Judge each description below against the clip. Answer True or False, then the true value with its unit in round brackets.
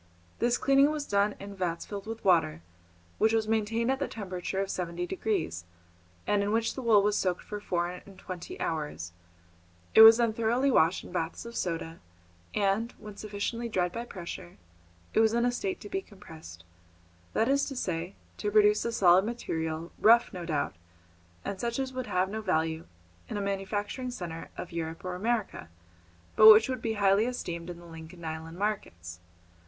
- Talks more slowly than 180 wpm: False (185 wpm)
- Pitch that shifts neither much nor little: True (4.7 semitones)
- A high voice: True (200 Hz)